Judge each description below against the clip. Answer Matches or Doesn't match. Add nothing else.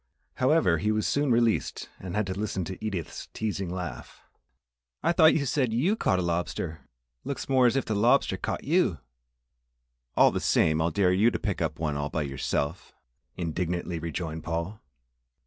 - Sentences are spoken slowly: Doesn't match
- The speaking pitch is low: Matches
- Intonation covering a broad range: Matches